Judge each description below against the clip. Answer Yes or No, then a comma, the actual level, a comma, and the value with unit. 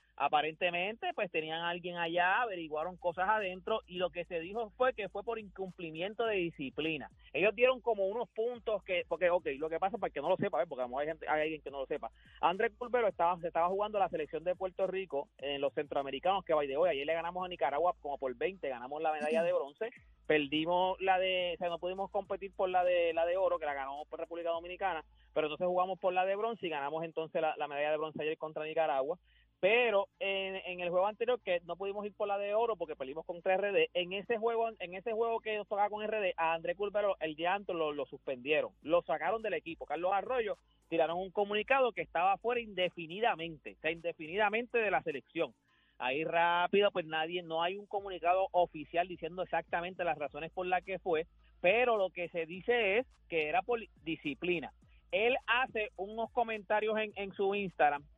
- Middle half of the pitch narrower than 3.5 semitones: No, average, 4.0 semitones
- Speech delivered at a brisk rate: Yes, fast, 220 wpm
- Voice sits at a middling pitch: Yes, medium, 180 Hz